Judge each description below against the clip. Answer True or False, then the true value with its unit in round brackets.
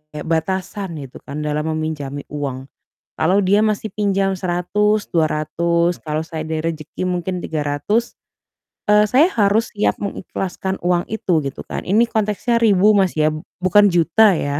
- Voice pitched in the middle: True (180 Hz)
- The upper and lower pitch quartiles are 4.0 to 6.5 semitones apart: True (4.6 semitones)